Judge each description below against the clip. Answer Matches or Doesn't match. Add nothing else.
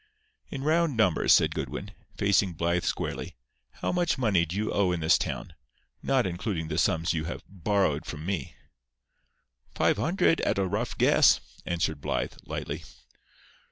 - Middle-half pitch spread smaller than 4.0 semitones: Doesn't match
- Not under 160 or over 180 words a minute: Doesn't match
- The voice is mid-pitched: Doesn't match